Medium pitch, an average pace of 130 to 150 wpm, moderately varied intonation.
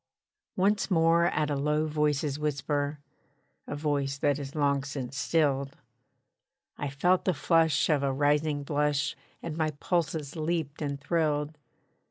No: medium, 150 Hz; average, 140 wpm; narrow, 2.0 semitones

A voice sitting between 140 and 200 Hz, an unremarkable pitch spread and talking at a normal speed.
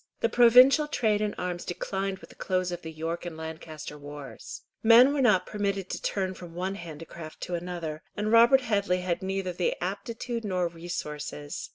Yes: medium, 185 Hz; average, 4.2 semitones; average, 175 wpm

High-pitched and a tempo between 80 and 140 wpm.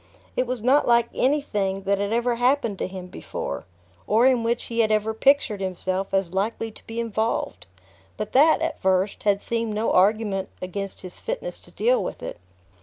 No: high, 220 Hz; average, 185 wpm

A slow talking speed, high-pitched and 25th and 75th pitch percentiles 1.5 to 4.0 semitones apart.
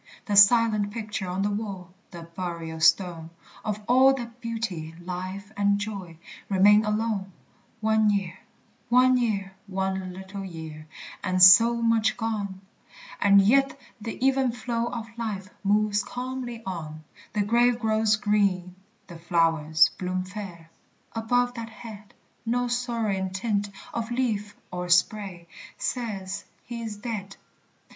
Yes: slow, 130 wpm; high, 205 Hz; average, 3.6 semitones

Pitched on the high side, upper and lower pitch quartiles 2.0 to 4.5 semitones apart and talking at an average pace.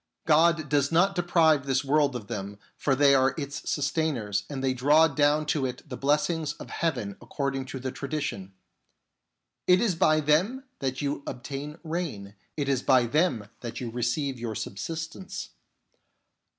No: medium, 140 Hz; average, 3.6 semitones; average, 165 wpm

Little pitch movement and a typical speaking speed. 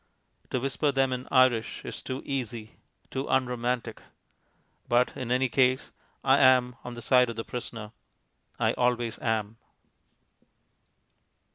No: narrow, 1.7 semitones; slow, 130 wpm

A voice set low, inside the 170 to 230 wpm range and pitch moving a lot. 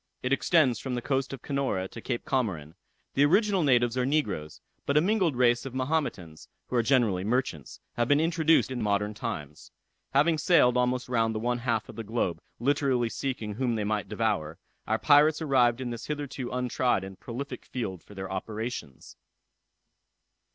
No: low, 125 Hz; average, 175 wpm; average, 4.3 semitones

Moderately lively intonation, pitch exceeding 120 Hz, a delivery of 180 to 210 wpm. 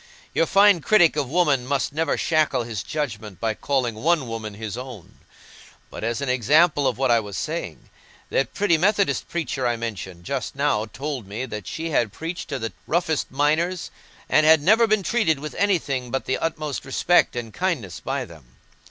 No: wide, 5.9 semitones; medium, 140 Hz; average, 185 wpm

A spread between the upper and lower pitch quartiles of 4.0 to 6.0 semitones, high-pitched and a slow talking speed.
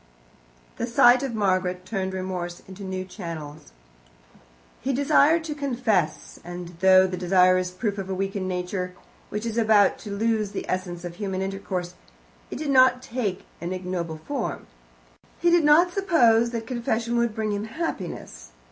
No: average, 4.4 semitones; high, 200 Hz; average, 160 wpm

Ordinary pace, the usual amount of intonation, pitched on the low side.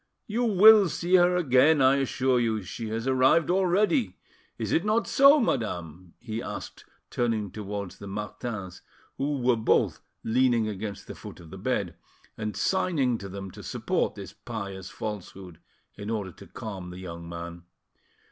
No: average, 160 wpm; wide, 7.1 semitones; low, 115 Hz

